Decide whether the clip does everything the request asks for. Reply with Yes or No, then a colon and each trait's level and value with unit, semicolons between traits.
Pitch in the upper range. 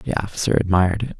No: very low, 95 Hz